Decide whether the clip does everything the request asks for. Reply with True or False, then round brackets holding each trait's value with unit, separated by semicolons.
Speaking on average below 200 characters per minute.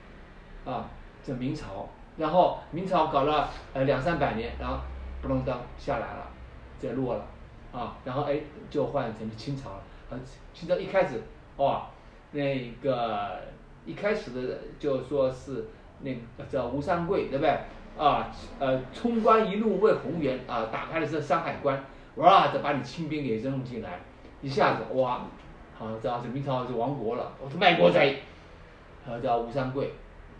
False (225 characters per minute)